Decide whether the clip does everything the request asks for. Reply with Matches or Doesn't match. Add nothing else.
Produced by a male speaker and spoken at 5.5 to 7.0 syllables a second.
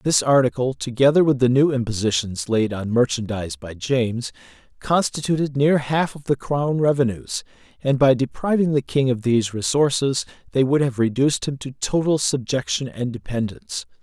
Doesn't match